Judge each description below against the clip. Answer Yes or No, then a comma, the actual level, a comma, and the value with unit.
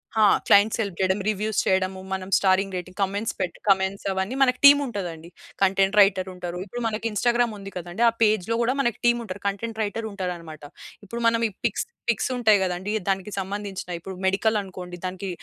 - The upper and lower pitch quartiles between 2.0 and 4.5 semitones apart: Yes, average, 2.8 semitones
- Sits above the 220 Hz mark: No, high, 195 Hz